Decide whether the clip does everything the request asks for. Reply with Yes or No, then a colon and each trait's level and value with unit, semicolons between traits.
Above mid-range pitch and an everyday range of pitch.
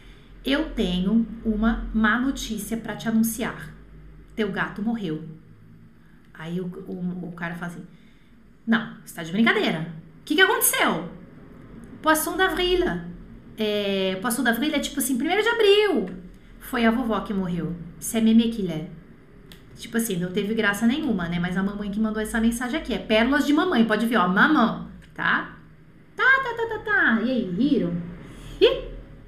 No: high, 220 Hz; wide, 5.7 semitones